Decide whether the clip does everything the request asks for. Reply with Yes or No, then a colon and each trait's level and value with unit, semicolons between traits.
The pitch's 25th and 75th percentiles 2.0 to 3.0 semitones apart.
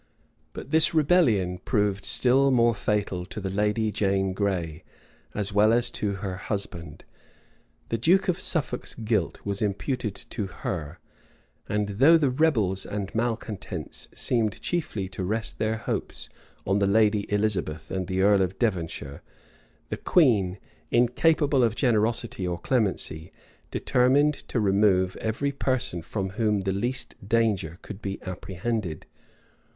No: average, 3.9 semitones